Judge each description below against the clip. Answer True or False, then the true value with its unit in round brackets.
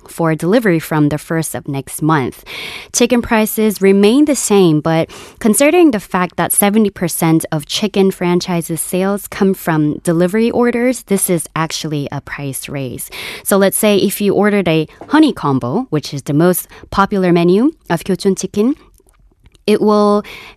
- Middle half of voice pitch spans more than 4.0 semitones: True (4.6 semitones)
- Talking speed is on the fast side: False (155 wpm)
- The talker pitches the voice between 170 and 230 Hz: True (185 Hz)